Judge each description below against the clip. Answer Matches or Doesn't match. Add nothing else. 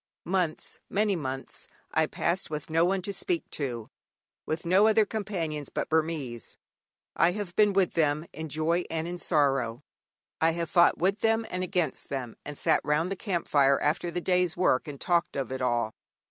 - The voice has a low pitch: Doesn't match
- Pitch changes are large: Doesn't match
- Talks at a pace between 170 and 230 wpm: Matches